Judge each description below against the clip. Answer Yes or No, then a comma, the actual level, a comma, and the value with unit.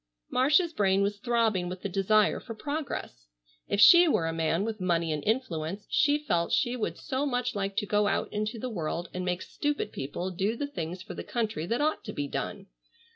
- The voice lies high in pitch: Yes, high, 205 Hz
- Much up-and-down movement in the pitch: Yes, wide, 5.8 semitones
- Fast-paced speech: Yes, fast, 210 wpm